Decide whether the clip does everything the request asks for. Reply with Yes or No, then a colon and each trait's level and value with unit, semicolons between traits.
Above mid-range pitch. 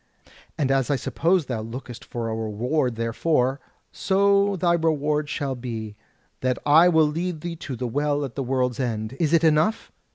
No: medium, 140 Hz